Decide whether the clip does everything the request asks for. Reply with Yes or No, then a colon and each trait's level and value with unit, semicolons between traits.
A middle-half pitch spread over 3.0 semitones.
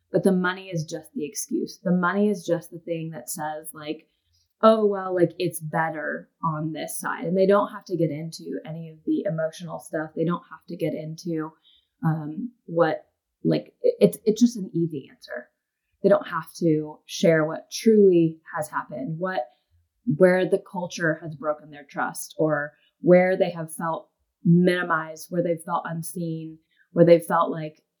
No: average, 2.7 semitones